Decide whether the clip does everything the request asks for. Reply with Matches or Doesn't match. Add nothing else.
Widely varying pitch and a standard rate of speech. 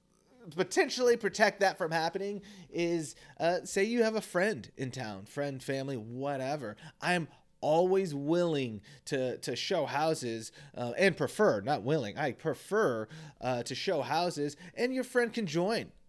Matches